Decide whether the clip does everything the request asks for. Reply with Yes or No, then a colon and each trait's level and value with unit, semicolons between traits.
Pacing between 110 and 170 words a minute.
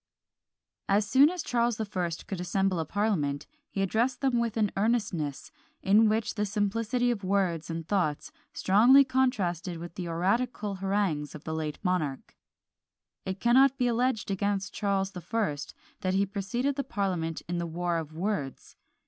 Yes: average, 165 wpm